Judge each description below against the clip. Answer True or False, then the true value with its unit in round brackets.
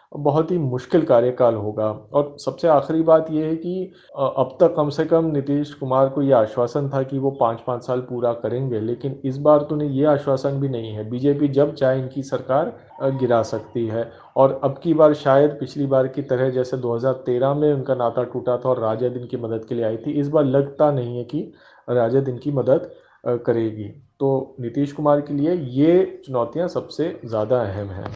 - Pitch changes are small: False (3.2 semitones)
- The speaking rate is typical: False (200 wpm)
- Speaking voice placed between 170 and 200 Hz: False (135 Hz)